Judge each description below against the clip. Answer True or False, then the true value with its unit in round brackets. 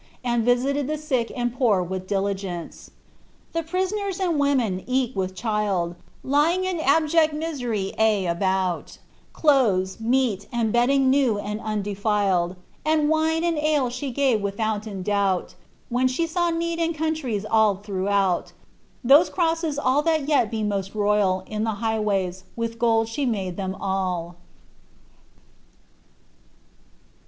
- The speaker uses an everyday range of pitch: False (6.6 semitones)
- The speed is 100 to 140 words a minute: True (135 wpm)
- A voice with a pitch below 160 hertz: False (230 Hz)